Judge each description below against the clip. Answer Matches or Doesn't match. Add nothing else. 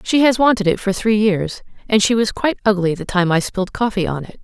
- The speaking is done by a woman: Matches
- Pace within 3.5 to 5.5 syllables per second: Doesn't match